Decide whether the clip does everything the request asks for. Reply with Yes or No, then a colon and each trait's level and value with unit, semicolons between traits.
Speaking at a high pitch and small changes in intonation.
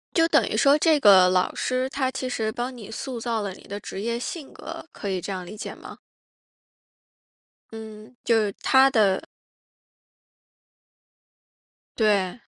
No: high, 225 Hz; average, 4.3 semitones